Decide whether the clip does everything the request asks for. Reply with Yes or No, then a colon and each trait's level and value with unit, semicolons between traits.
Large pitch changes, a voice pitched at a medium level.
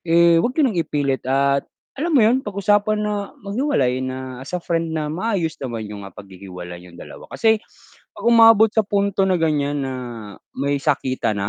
Yes: wide, 8.0 semitones; medium, 165 Hz